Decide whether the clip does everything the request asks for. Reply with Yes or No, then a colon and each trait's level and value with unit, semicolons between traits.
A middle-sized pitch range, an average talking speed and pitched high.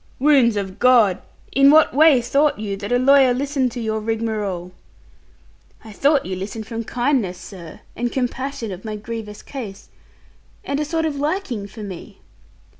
Yes: average, 4.9 semitones; average, 170 wpm; high, 235 Hz